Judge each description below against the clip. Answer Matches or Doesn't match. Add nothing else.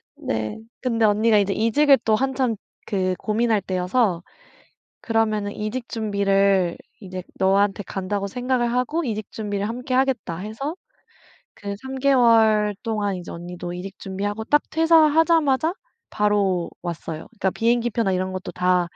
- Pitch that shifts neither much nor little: Matches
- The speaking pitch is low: Doesn't match